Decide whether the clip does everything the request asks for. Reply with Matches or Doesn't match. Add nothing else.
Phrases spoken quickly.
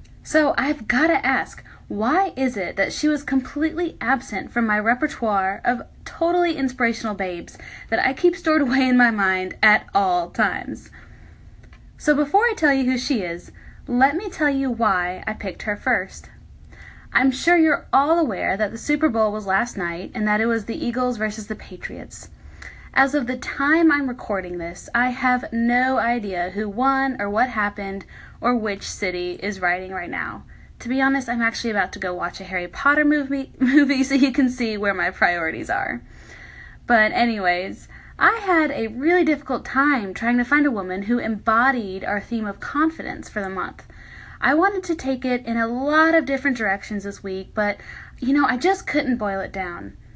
Doesn't match